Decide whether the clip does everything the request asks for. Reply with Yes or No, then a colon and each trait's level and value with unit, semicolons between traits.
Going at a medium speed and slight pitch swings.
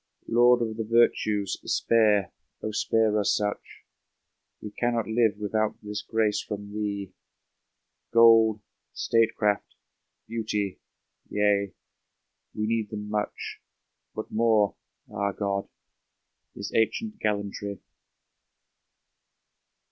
No: slow, 100 wpm; narrow, 1.6 semitones